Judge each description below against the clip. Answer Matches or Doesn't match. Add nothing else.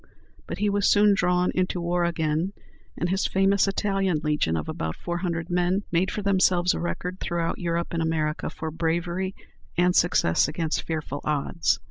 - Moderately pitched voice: Matches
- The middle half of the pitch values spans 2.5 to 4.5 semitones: Matches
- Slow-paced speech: Doesn't match